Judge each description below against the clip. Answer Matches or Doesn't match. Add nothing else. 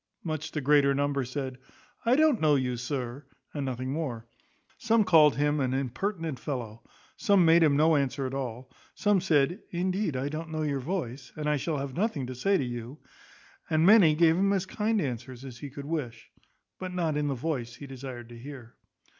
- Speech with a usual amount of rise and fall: Matches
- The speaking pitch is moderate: Matches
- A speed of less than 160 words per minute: Doesn't match